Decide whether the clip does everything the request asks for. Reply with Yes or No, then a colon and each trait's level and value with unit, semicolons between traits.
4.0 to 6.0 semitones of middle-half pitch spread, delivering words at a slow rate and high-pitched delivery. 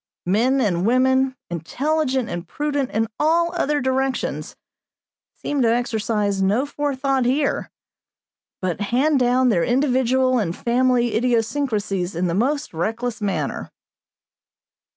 Yes: average, 4.3 semitones; slow, 115 wpm; high, 245 Hz